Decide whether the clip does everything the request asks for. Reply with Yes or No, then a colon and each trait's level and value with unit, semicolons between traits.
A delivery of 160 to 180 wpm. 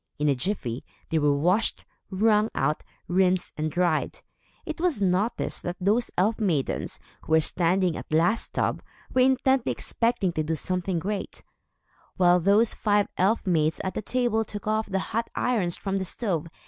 Yes: average, 175 wpm